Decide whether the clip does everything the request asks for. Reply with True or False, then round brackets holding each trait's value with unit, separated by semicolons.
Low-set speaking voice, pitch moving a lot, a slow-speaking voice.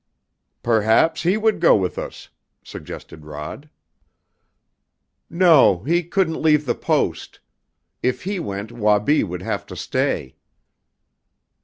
True (125 Hz; 8.7 semitones; 115 wpm)